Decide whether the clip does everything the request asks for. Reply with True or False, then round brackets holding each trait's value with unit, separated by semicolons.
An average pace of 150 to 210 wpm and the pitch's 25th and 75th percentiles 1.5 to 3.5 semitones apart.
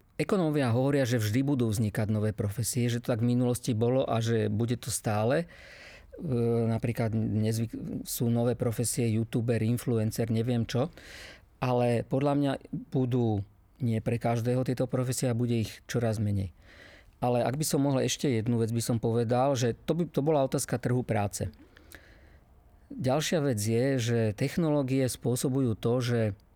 True (155 wpm; 2.6 semitones)